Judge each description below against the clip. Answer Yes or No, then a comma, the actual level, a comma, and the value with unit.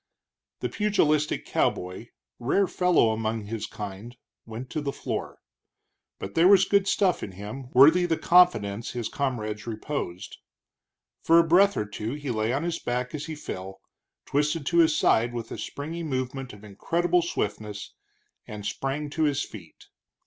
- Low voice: Yes, low, 130 Hz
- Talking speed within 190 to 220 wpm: No, average, 160 wpm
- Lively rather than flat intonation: Yes, wide, 7.0 semitones